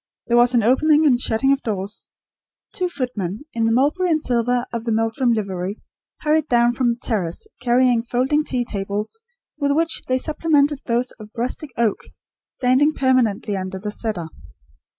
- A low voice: No, high, 240 Hz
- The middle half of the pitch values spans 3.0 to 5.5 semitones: Yes, average, 3.9 semitones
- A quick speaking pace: No, average, 165 wpm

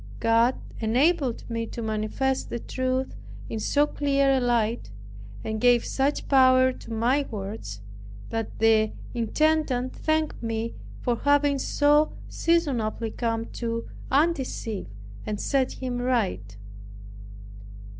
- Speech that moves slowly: Yes, slow, 115 wpm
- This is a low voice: No, high, 245 Hz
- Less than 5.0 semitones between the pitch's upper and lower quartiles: Yes, average, 3.5 semitones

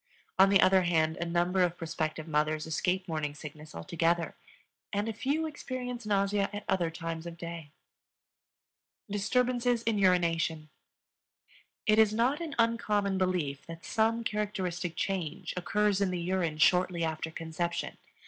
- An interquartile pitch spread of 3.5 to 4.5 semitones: Yes, average, 4.2 semitones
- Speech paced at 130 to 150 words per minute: Yes, average, 140 wpm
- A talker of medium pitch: Yes, medium, 180 Hz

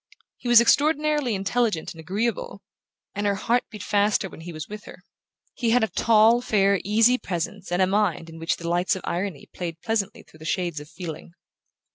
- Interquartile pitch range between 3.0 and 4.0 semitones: No, average, 4.8 semitones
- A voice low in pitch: No, high, 200 Hz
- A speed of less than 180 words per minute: No, average, 195 wpm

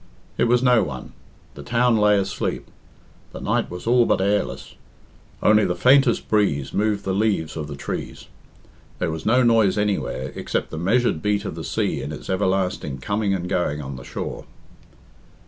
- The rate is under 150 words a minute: No, average, 175 wpm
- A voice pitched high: No, low, 100 Hz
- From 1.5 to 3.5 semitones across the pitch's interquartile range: No, wide, 5.5 semitones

